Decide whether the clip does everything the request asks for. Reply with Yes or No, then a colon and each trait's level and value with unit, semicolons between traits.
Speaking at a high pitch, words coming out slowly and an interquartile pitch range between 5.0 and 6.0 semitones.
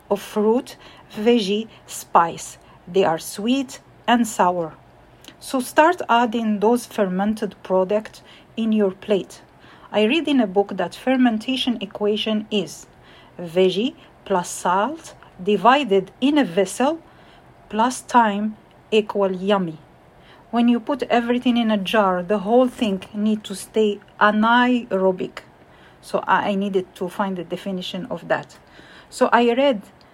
No: high, 215 Hz; slow, 125 wpm; average, 3.4 semitones